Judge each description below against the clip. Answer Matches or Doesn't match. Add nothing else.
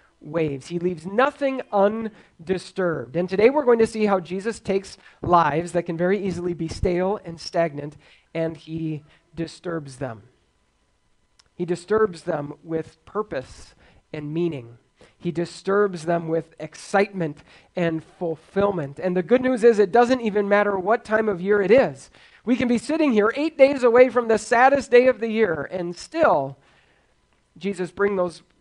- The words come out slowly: Doesn't match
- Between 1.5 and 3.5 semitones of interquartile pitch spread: Doesn't match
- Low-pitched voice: Doesn't match